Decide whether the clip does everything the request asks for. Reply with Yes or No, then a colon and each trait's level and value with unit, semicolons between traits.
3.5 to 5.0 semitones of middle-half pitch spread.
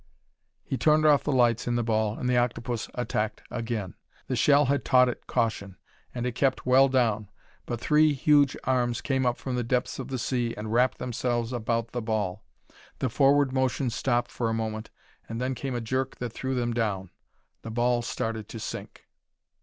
No: narrow, 2.5 semitones